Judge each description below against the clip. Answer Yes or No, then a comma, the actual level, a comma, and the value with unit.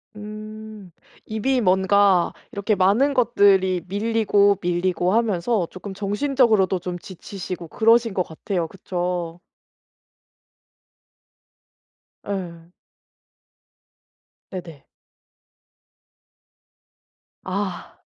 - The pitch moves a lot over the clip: No, average, 3.1 semitones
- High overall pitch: Yes, high, 195 Hz